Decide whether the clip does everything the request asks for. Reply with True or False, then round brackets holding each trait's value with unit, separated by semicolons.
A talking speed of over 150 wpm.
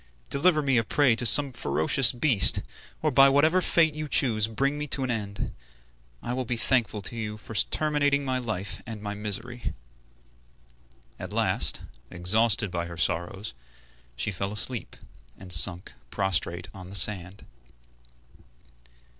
False (145 wpm)